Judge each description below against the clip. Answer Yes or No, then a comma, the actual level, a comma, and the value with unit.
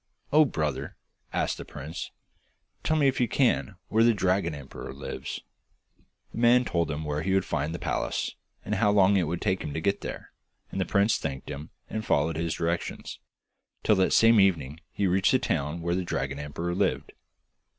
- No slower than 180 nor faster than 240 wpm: Yes, average, 190 wpm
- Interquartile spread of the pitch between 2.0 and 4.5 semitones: No, average, 5.1 semitones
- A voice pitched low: Yes, very low, 90 Hz